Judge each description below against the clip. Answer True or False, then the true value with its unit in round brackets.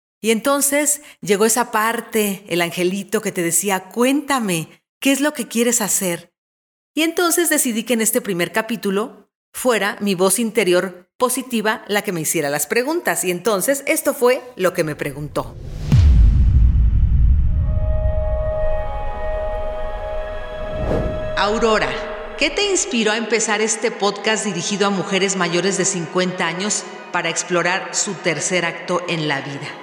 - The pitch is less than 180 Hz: False (195 Hz)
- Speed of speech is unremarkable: True (135 wpm)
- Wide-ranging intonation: True (5.7 semitones)